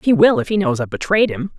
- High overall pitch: Yes, high, 195 Hz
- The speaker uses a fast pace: Yes, fast, 305 wpm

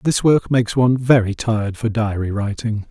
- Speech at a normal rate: Yes, average, 185 wpm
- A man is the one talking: Yes, male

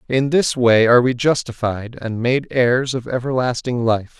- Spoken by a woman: No, male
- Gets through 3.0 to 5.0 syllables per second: Yes, 4.5 syllables/s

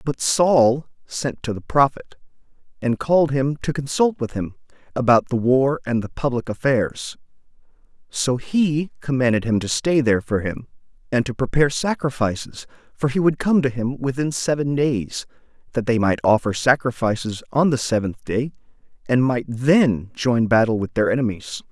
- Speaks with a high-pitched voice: No, low, 130 Hz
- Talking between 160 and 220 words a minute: Yes, average, 165 wpm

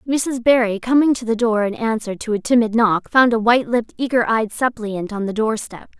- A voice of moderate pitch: No, high, 225 Hz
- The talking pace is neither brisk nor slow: No, fast, 220 wpm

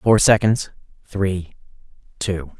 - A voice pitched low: Yes, very low, 95 Hz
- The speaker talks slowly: Yes, slow, 95 wpm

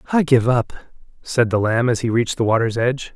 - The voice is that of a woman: No, male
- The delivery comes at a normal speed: No, fast, 230 wpm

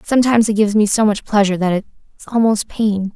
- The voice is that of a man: No, female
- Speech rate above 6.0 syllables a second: Yes, 7.0 syllables/s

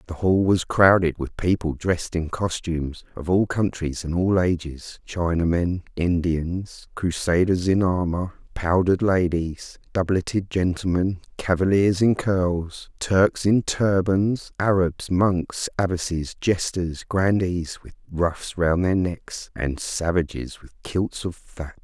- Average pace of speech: No, slow, 125 wpm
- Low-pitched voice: Yes, very low, 90 Hz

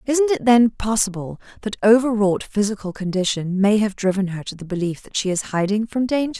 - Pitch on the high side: Yes, high, 210 Hz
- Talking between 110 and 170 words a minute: No, fast, 205 wpm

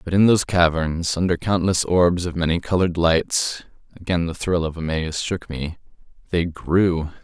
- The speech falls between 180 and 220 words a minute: No, average, 150 wpm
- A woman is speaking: No, male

